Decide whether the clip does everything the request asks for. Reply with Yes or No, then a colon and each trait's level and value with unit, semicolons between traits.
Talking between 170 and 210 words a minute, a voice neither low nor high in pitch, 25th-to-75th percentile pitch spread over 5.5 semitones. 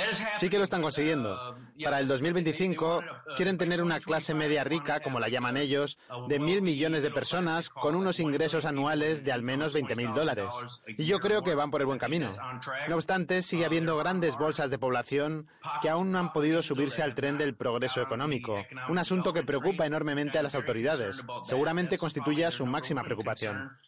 No: average, 185 wpm; medium, 150 Hz; average, 3.4 semitones